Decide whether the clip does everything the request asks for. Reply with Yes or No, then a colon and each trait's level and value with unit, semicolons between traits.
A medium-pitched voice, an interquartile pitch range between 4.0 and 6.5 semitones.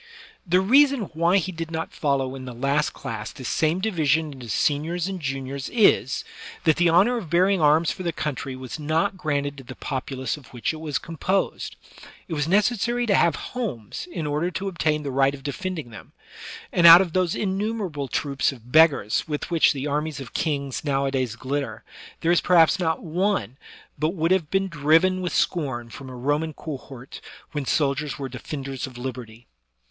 Yes: medium, 155 Hz; average, 4.5 semitones